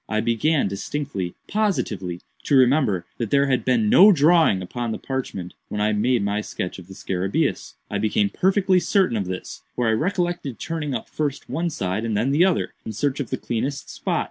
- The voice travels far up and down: Yes, wide, 6.6 semitones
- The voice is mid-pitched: No, low, 120 Hz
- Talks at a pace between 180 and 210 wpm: Yes, average, 195 wpm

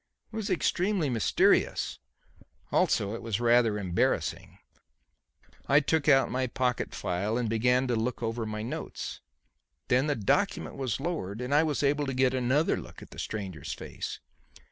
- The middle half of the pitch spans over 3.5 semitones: Yes, average, 4.3 semitones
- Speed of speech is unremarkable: Yes, average, 160 wpm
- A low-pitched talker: Yes, low, 125 Hz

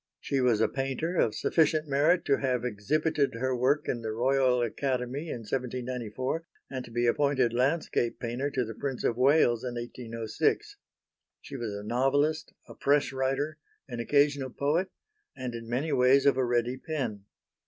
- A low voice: Yes, low, 130 Hz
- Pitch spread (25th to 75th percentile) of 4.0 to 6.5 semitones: No, average, 3.0 semitones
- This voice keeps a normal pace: Yes, average, 165 wpm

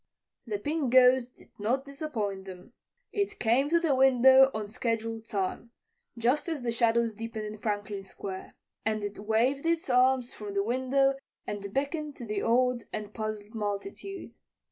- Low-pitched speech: No, high, 235 Hz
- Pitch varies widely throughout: No, average, 4.1 semitones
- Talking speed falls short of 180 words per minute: Yes, average, 160 wpm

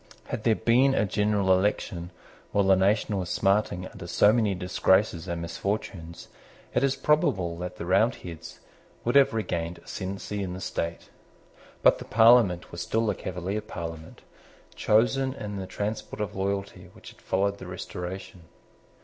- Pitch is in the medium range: No, low, 100 Hz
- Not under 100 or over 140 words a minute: No, average, 155 wpm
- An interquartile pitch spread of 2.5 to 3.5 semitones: Yes, average, 3.1 semitones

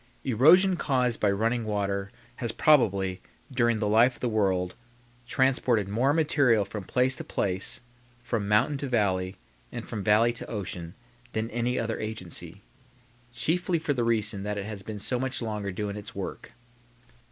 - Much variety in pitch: No, average, 3.8 semitones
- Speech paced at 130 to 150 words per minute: No, average, 165 wpm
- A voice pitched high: No, low, 110 Hz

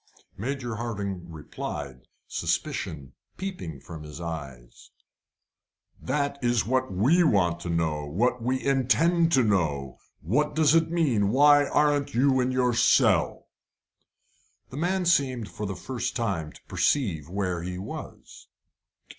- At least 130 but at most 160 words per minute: Yes, slow, 135 wpm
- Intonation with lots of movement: Yes, wide, 8.4 semitones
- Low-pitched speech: Yes, low, 115 Hz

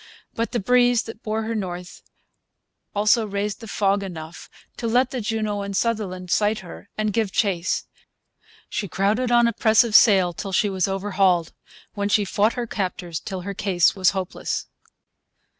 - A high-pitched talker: Yes, high, 205 Hz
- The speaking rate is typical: Yes, average, 170 wpm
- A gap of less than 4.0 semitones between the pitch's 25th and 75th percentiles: Yes, average, 2.8 semitones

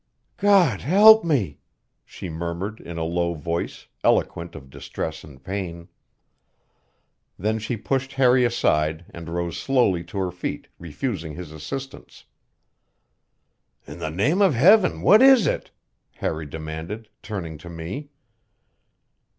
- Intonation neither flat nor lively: No, wide, 8.3 semitones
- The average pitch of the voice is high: No, very low, 90 Hz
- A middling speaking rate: No, slow, 125 wpm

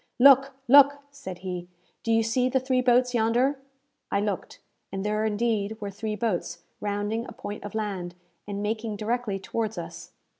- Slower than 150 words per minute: No, average, 165 wpm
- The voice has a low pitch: No, high, 220 Hz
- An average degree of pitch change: Yes, average, 3.3 semitones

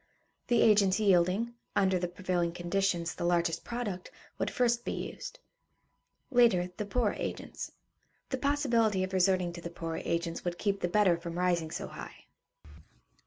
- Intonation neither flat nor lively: Yes, average, 3.8 semitones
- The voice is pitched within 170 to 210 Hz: Yes, medium, 185 Hz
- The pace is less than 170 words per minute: Yes, average, 155 wpm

